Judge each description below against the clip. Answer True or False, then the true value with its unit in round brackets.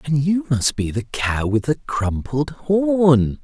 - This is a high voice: False (135 Hz)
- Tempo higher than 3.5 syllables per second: False (3.4 syllables/s)